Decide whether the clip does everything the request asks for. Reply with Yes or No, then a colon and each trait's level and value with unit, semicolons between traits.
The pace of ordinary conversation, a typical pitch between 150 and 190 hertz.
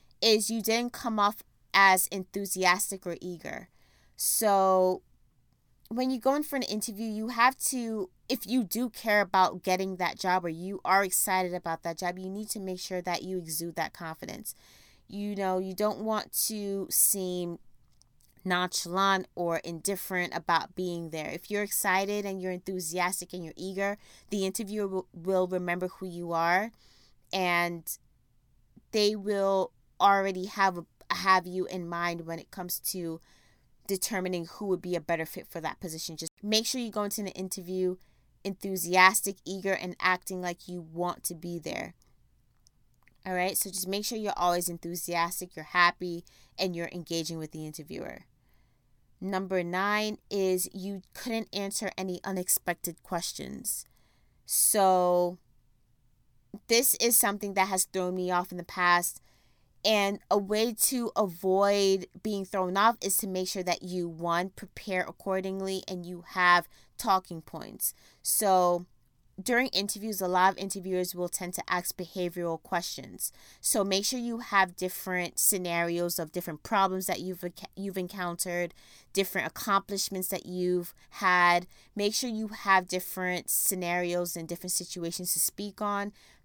Yes: average, 150 wpm; medium, 185 Hz